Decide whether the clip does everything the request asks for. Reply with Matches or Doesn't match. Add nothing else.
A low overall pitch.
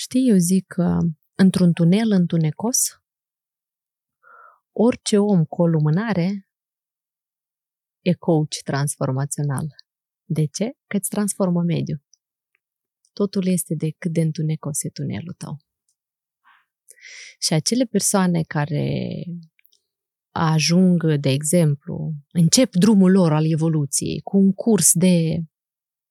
Doesn't match